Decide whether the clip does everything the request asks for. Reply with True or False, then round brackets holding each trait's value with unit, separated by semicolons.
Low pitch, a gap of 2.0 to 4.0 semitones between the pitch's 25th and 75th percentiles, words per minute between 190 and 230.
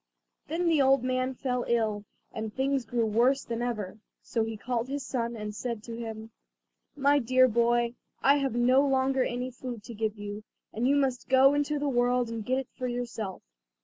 False (245 Hz; 2.7 semitones; 195 wpm)